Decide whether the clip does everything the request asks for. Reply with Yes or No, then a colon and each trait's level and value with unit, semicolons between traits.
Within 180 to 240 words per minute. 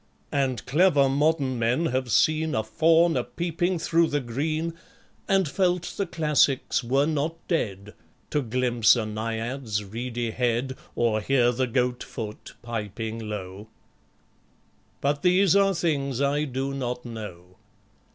No: slow, 135 wpm